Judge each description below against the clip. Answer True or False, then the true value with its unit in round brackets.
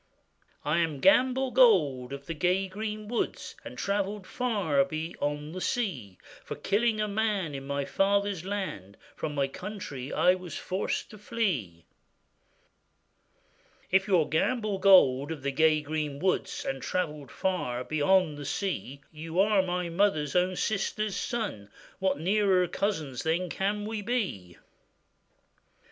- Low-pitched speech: False (180 Hz)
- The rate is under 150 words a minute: True (140 wpm)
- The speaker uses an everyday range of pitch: False (5.7 semitones)